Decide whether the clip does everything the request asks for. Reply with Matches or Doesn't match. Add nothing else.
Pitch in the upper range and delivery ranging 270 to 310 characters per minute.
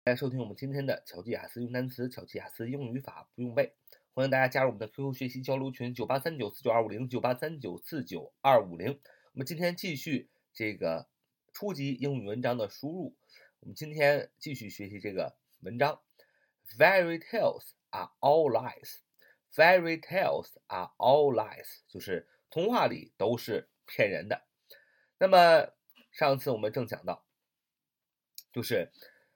Doesn't match